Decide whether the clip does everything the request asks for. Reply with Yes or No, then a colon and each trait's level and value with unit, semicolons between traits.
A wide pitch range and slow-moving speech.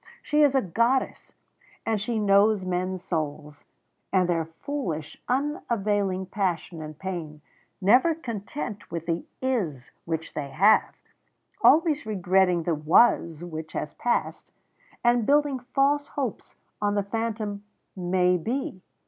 Yes: wide, 5.8 semitones; slow, 125 wpm